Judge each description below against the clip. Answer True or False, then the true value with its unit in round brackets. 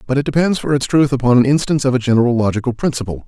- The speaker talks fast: True (255 wpm)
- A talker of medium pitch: False (130 Hz)